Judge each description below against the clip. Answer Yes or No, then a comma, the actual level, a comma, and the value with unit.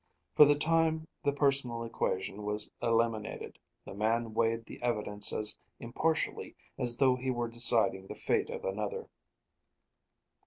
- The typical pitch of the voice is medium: No, low, 120 Hz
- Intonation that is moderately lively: Yes, average, 4.6 semitones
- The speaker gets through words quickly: No, average, 140 wpm